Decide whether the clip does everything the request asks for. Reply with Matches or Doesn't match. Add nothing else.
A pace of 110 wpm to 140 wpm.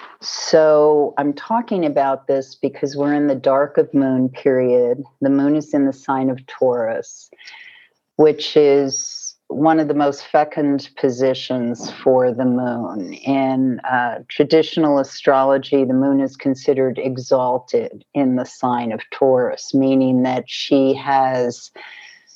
Matches